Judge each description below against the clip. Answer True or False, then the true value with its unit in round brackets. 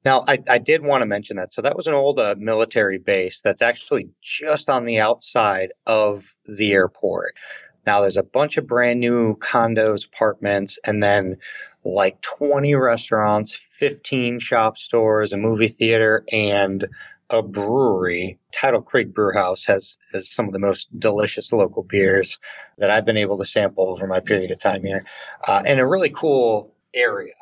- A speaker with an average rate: True (170 wpm)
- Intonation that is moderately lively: True (3.3 semitones)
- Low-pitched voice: True (110 Hz)